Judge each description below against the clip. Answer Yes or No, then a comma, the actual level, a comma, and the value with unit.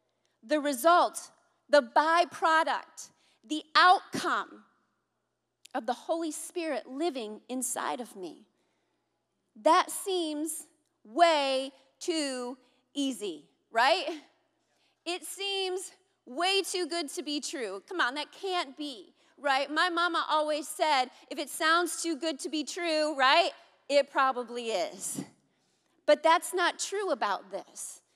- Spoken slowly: Yes, slow, 120 wpm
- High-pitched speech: Yes, very high, 320 Hz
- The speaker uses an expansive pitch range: No, average, 3.2 semitones